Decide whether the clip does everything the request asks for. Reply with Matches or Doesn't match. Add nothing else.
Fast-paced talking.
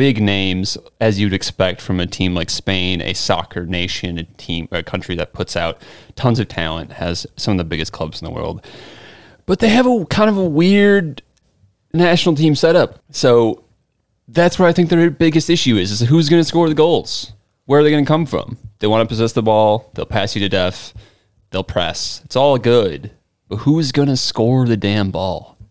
Matches